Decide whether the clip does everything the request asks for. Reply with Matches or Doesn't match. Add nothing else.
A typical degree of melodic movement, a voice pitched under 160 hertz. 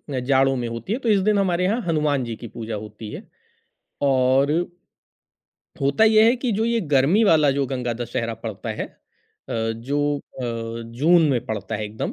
Doesn't match